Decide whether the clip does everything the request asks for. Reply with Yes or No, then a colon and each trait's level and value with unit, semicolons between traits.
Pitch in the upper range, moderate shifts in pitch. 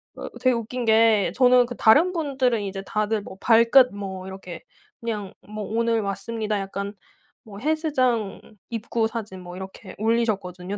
Yes: high, 220 Hz; average, 3.1 semitones